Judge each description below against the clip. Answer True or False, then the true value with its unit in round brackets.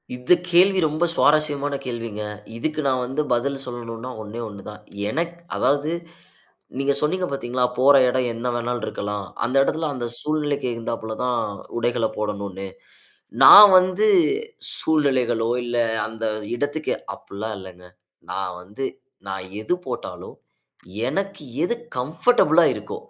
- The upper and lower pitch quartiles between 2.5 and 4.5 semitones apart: False (5.1 semitones)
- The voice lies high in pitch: False (125 Hz)